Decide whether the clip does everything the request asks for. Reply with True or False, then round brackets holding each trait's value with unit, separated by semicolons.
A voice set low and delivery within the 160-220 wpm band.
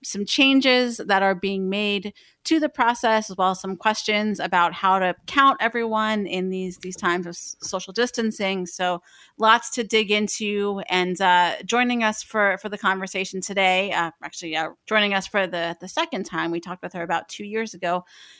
False (195 Hz; 190 wpm)